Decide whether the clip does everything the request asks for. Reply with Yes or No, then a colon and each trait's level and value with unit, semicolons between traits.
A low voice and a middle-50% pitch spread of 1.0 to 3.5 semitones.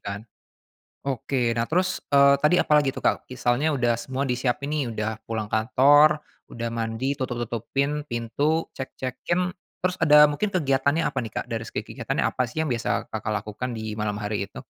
No: low, 130 Hz; average, 4.4 semitones